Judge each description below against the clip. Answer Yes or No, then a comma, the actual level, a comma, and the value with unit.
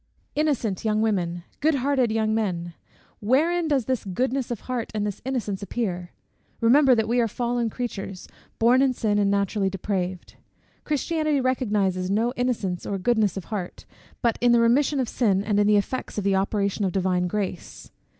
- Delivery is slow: No, average, 175 wpm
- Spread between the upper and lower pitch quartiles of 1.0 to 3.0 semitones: No, average, 4.2 semitones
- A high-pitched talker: Yes, high, 220 Hz